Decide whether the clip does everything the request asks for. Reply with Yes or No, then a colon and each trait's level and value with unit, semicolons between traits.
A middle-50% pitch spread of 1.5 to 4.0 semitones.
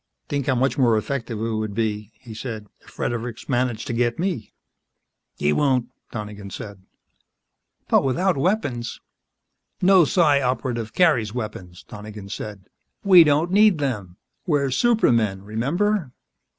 No: average, 5.2 semitones